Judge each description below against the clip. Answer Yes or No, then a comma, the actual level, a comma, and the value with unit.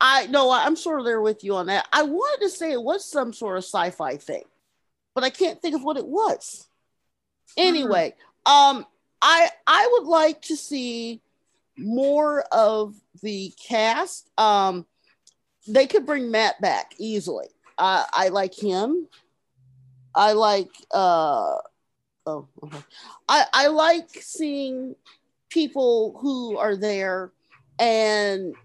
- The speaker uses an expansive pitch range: Yes, wide, 7.6 semitones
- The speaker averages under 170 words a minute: Yes, average, 140 wpm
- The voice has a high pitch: Yes, very high, 260 Hz